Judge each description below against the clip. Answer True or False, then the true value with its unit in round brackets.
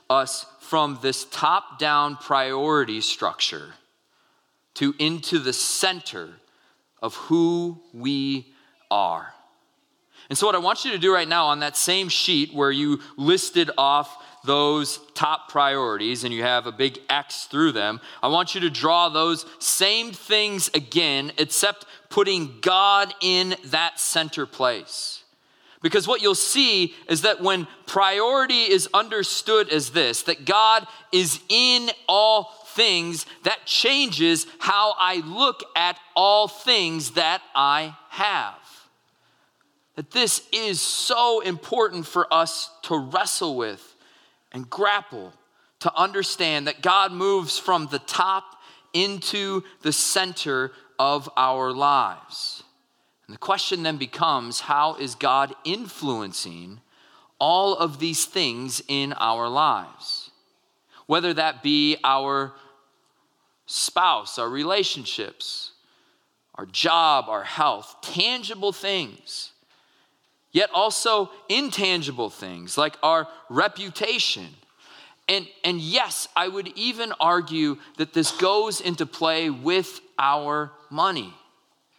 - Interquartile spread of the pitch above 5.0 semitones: True (5.4 semitones)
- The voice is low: False (170 Hz)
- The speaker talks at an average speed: False (120 wpm)